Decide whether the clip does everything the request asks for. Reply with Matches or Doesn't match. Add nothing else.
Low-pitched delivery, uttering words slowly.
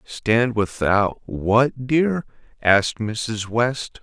Matches